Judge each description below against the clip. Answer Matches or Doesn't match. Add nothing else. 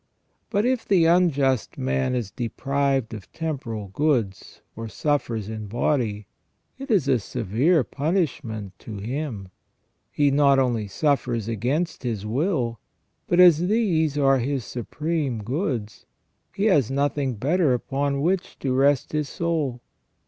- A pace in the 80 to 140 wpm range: Matches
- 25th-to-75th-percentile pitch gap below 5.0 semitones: Doesn't match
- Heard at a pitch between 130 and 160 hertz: Matches